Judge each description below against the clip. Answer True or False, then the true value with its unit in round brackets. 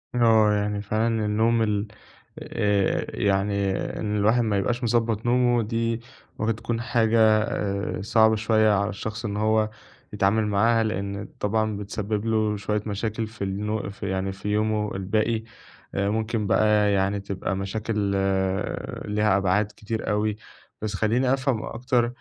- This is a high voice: False (110 Hz)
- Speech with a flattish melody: True (1.8 semitones)